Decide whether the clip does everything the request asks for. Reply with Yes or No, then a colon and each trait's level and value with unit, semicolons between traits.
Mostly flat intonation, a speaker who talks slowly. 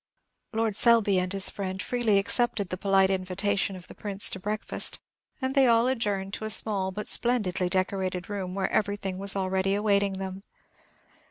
No: narrow, 2.1 semitones; average, 170 wpm